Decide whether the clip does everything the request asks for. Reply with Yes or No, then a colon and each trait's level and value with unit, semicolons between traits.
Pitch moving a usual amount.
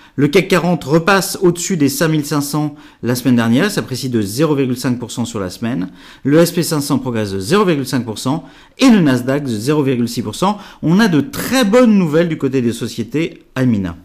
No: wide, 5.7 semitones